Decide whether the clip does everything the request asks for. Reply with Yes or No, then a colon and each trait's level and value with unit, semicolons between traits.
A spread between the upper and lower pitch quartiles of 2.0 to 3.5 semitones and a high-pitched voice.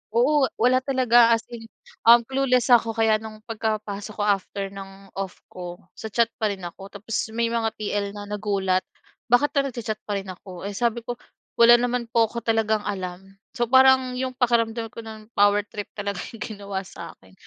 Yes: average, 2.9 semitones; high, 220 Hz